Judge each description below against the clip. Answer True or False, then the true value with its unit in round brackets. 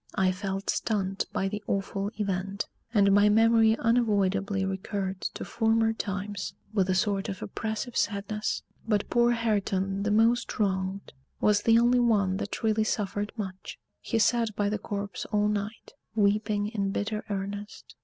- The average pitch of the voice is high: True (205 Hz)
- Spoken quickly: False (155 wpm)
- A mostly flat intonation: True (2.0 semitones)